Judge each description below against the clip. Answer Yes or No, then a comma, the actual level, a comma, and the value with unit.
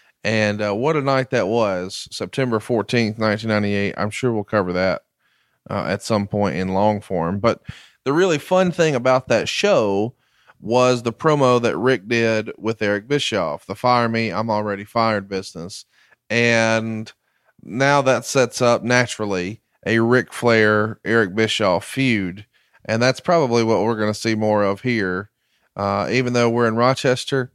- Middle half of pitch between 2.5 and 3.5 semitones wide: Yes, average, 3.1 semitones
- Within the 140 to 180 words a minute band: Yes, average, 165 wpm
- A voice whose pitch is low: Yes, low, 115 Hz